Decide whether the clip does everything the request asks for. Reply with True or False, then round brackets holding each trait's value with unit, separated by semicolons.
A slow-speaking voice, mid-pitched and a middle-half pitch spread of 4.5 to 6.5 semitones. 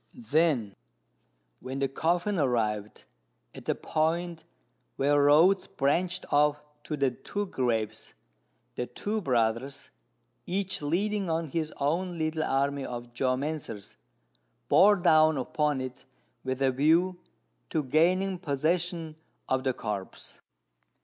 True (115 wpm; 150 Hz; 4.8 semitones)